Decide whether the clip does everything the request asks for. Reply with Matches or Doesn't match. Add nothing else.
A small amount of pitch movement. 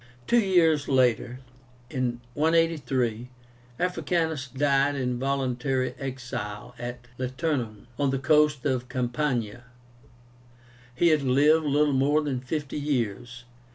Doesn't match